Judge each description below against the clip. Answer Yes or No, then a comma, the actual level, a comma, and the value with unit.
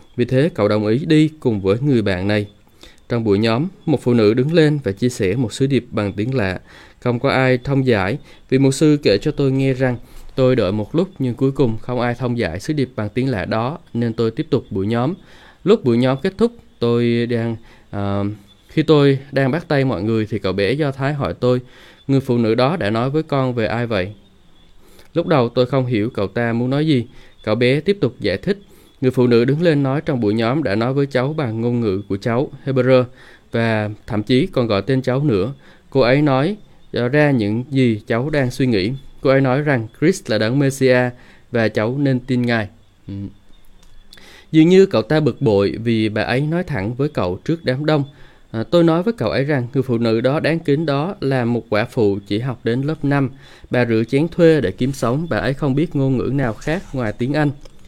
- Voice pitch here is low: Yes, low, 125 Hz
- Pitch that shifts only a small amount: No, average, 3.9 semitones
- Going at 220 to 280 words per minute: Yes, average, 230 wpm